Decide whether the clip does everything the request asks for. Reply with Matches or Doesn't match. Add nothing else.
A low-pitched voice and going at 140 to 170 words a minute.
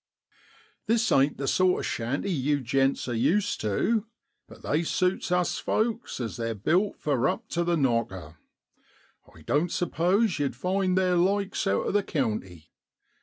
Doesn't match